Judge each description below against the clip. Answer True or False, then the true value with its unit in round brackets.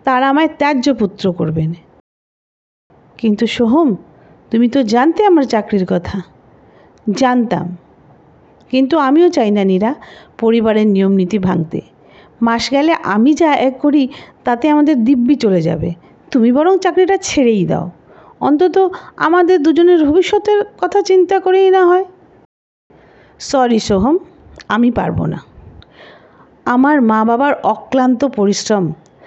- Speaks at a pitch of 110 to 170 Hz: False (255 Hz)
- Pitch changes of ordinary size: False (7.9 semitones)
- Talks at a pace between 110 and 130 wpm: True (115 wpm)